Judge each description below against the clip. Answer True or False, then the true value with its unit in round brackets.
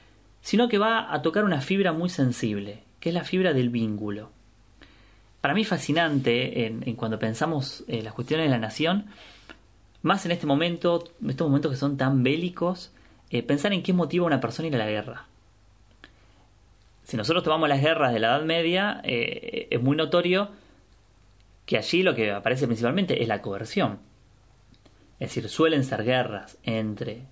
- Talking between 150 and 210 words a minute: True (175 wpm)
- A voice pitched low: True (125 Hz)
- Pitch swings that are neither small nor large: False (7.7 semitones)